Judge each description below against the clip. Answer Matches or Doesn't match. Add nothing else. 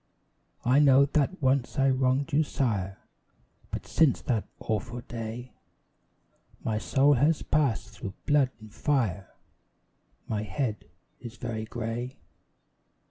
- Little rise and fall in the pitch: Doesn't match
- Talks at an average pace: Doesn't match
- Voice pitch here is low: Matches